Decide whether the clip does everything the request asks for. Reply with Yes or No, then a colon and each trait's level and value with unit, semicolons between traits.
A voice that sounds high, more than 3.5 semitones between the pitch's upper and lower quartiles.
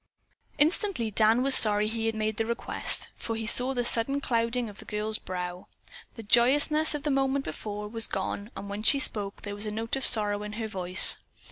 No: high, 225 Hz; average, 3.2 semitones